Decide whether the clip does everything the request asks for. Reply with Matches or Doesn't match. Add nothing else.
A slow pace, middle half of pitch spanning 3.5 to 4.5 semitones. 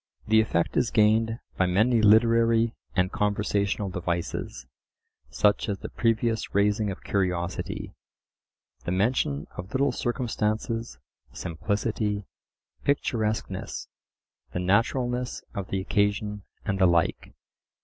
Doesn't match